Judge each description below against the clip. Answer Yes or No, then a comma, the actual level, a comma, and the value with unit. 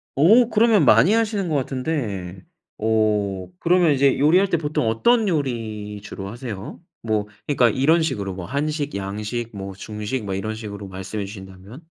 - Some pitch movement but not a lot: No, wide, 7.1 semitones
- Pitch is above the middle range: No, low, 115 Hz